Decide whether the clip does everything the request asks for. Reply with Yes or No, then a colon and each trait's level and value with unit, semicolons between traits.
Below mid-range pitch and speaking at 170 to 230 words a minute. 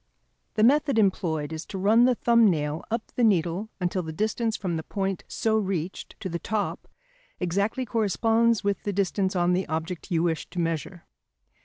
No: high, 195 Hz; average, 180 wpm